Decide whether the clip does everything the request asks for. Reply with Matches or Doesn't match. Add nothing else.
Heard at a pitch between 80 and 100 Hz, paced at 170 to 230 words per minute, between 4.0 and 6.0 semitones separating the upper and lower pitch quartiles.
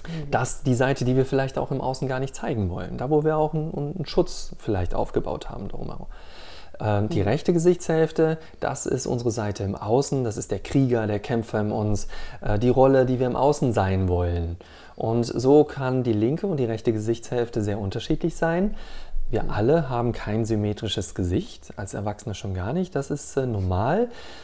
Doesn't match